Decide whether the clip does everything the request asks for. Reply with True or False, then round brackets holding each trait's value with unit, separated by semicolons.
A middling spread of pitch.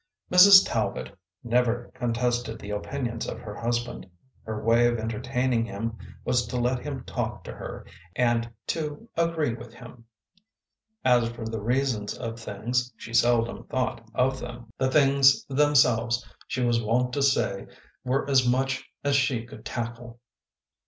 False (2.2 semitones)